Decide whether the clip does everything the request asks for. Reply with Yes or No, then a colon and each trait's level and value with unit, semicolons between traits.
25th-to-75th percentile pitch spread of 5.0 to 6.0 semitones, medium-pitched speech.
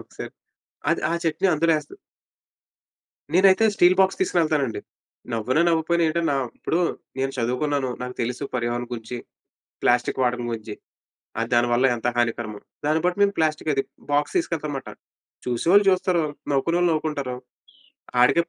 Yes: wide, 5.5 semitones; medium, 145 Hz